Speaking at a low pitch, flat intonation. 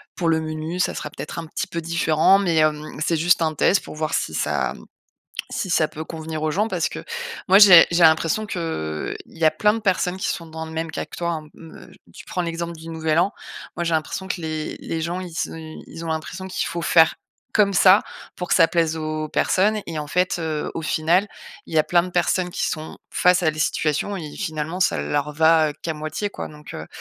No: medium, 165 Hz; narrow, 2.3 semitones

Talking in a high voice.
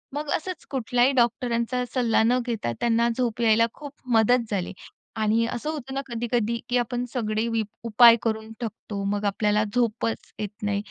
Yes: high, 235 Hz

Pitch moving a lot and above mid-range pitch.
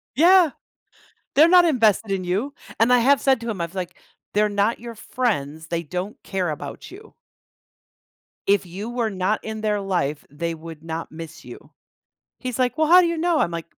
Yes: wide, 7.0 semitones; high, 210 Hz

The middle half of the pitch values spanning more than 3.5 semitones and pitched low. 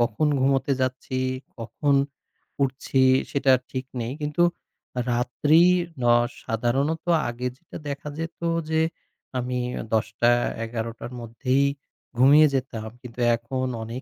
No: average, 2.9 semitones; low, 130 Hz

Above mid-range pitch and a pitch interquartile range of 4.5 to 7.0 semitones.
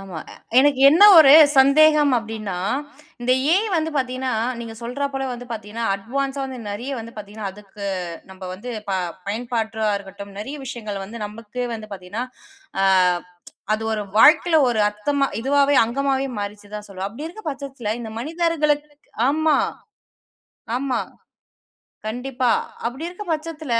Yes: very high, 250 Hz; average, 5.1 semitones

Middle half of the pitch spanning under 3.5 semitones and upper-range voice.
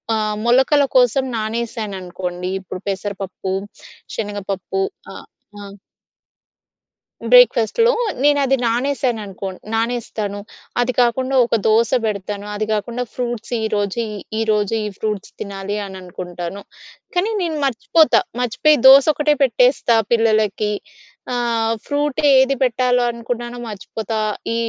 No: average, 3.8 semitones; high, 225 Hz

